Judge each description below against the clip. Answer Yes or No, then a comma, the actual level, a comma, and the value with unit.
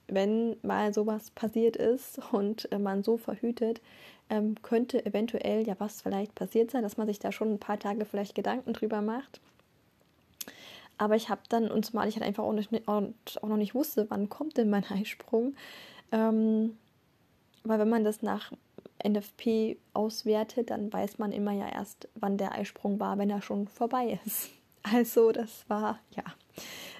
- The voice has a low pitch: No, high, 215 Hz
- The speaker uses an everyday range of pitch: No, narrow, 1.7 semitones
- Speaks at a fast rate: No, average, 165 wpm